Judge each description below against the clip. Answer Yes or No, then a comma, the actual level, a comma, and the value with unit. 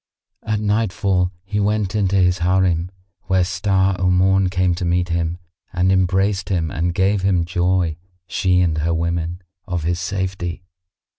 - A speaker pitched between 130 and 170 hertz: No, very low, 90 Hz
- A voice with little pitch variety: Yes, narrow, 1.8 semitones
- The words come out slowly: No, average, 160 wpm